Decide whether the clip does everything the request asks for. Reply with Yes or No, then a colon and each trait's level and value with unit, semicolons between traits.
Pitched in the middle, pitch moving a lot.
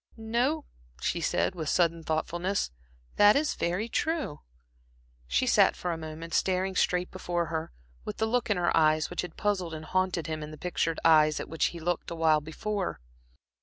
No: medium, 175 Hz; average, 3.4 semitones